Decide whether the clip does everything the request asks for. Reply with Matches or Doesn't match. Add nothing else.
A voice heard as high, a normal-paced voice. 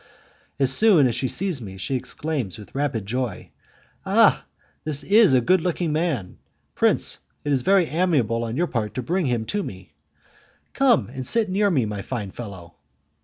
Doesn't match